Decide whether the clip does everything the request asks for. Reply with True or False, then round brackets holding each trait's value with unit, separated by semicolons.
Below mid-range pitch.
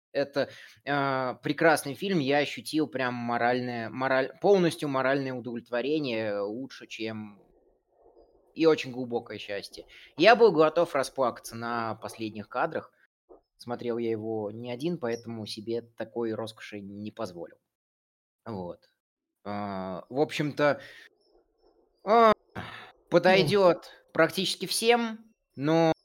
True (130 Hz)